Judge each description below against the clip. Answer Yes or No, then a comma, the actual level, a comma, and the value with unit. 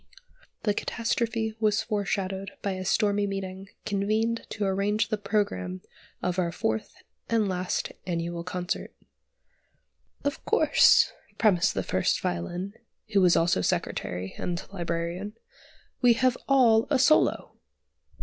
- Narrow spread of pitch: No, average, 3.7 semitones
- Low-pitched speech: No, high, 195 Hz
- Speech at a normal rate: No, slow, 120 wpm